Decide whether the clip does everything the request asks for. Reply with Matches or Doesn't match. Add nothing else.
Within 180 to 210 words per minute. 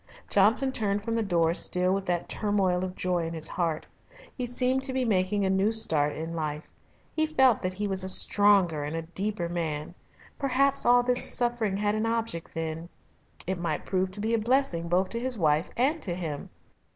Matches